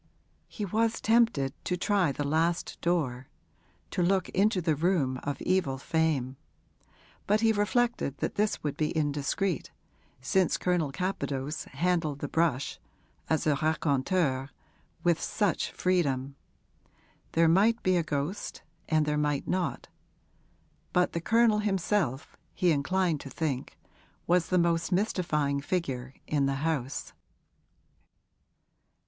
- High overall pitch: No, medium, 165 Hz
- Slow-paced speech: Yes, slow, 125 wpm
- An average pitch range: Yes, average, 4.7 semitones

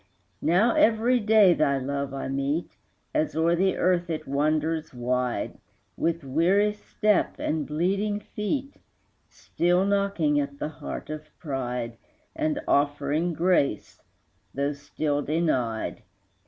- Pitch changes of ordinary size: No, wide, 5.8 semitones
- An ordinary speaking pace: No, slow, 120 wpm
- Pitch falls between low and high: Yes, medium, 160 Hz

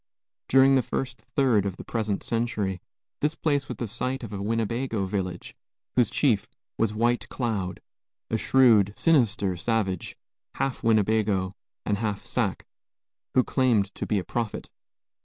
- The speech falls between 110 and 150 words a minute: Yes, average, 145 wpm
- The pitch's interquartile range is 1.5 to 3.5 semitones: No, average, 4.0 semitones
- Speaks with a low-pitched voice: Yes, low, 110 Hz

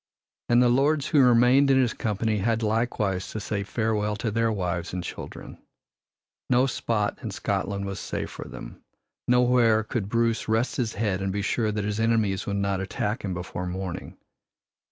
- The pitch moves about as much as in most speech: Yes, average, 3.2 semitones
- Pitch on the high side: No, low, 110 Hz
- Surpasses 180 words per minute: No, average, 175 wpm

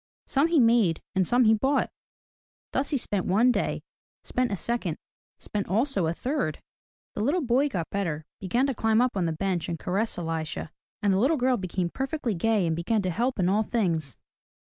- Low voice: No, high, 210 Hz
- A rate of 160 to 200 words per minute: Yes, average, 195 wpm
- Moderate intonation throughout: No, wide, 5.9 semitones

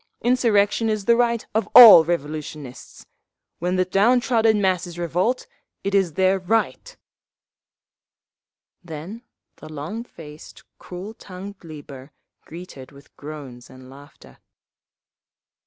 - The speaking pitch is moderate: Yes, medium, 180 Hz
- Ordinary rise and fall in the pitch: No, wide, 6.2 semitones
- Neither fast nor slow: No, slow, 110 wpm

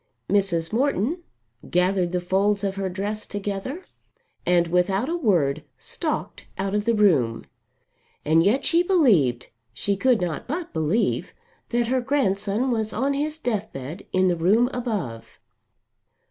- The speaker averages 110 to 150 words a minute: Yes, average, 140 wpm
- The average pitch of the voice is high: Yes, high, 200 Hz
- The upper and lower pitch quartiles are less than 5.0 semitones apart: No, wide, 5.5 semitones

